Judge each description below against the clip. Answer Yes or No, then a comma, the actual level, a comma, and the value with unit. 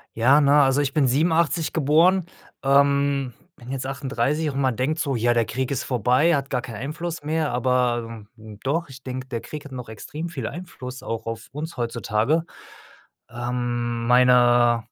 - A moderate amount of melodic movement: Yes, average, 3.5 semitones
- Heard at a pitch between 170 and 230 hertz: No, low, 130 Hz